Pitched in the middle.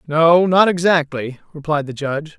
Yes: medium, 160 Hz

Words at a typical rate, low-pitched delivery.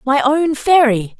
No: average, 150 wpm; very high, 275 Hz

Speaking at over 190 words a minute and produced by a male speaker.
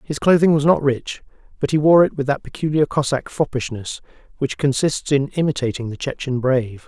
No: average, 185 wpm; male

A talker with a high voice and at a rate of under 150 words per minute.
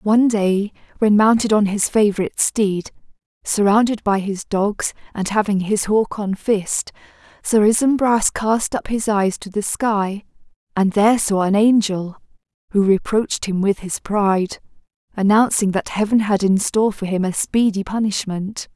No: high, 205 Hz; average, 155 wpm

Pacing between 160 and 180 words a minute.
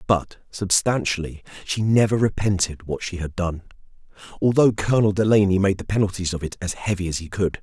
Yes: average, 175 wpm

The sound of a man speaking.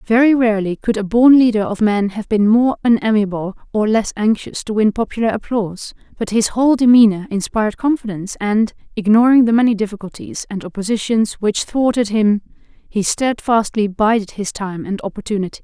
No: female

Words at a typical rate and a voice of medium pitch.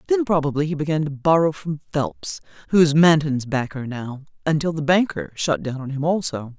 Yes: average, 180 wpm; medium, 150 Hz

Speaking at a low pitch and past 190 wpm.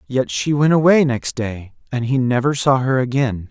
Yes: low, 130 Hz; fast, 205 wpm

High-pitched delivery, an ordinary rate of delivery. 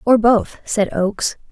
Yes: high, 215 Hz; average, 160 wpm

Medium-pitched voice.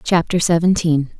Yes: medium, 165 Hz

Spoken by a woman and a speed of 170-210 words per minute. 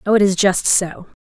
No: female; fast, 245 wpm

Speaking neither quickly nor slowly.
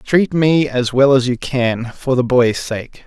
No: fast, 215 wpm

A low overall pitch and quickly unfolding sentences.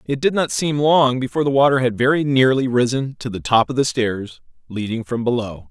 Yes: low, 125 Hz; fast, 220 wpm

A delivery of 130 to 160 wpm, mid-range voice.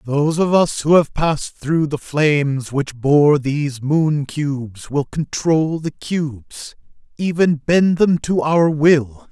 Yes: average, 155 wpm; medium, 150 Hz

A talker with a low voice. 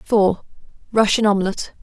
No: high, 205 Hz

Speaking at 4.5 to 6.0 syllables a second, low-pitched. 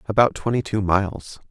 Yes: 5.5 syllables/s; low, 100 Hz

